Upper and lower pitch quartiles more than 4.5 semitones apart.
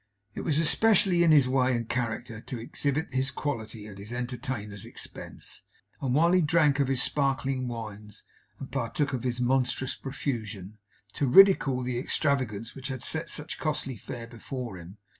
No: average, 3.5 semitones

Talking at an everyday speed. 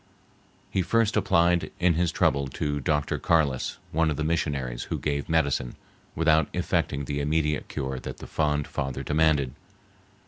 Yes: average, 150 wpm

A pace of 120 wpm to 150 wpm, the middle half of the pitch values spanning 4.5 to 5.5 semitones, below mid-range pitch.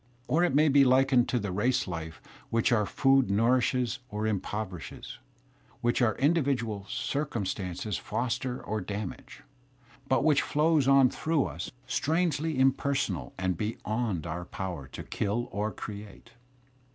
Yes: average, 140 wpm; average, 5.0 semitones; low, 120 Hz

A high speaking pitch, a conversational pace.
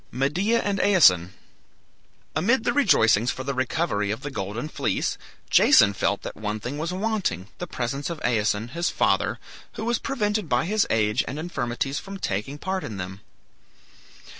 No: medium, 140 Hz; average, 165 wpm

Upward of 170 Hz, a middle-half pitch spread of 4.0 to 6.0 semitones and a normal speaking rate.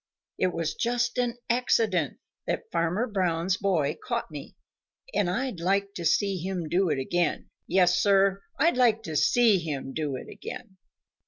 Yes: medium, 185 Hz; average, 4.3 semitones; average, 160 wpm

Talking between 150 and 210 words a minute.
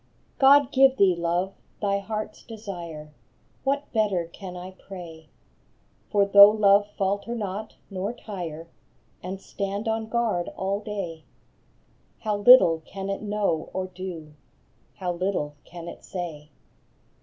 No: slow, 135 wpm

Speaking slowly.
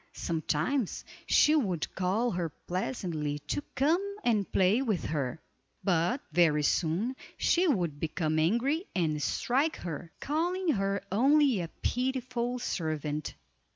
Yes: slow, 120 wpm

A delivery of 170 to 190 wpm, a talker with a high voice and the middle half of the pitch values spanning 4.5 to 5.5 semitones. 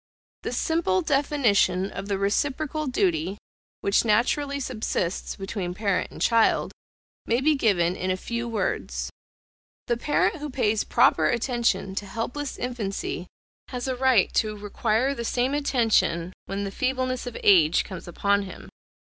No: average, 145 wpm; high, 225 Hz; average, 5.0 semitones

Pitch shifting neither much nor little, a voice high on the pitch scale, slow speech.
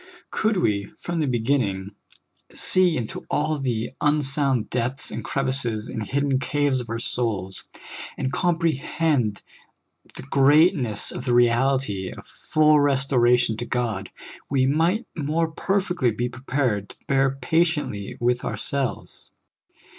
No: average, 3.9 semitones; low, 130 Hz; slow, 125 wpm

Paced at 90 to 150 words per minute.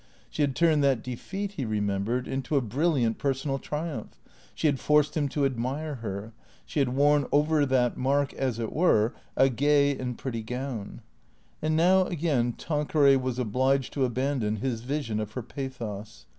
No: average, 170 wpm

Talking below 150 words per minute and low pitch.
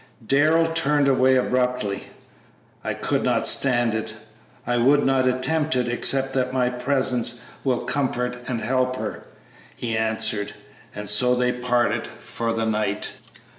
Yes: average, 140 wpm; low, 125 Hz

